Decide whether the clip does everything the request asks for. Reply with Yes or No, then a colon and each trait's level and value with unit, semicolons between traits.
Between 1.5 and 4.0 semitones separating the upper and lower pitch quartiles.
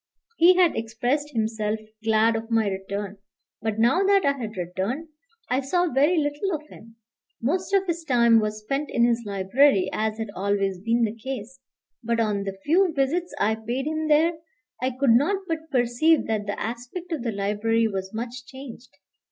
No: wide, 5.5 semitones